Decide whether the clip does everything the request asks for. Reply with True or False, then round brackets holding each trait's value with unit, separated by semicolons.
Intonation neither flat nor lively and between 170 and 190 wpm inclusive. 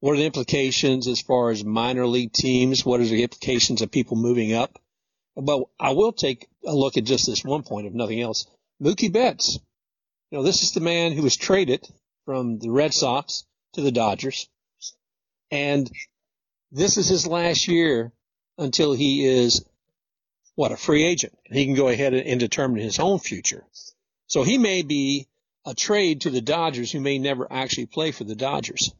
True (4.5 semitones; 185 wpm)